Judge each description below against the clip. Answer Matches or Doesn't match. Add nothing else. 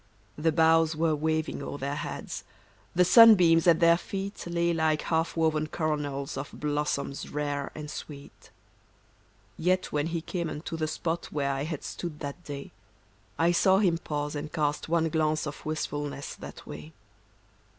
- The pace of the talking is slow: Doesn't match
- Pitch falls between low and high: Matches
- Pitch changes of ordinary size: Doesn't match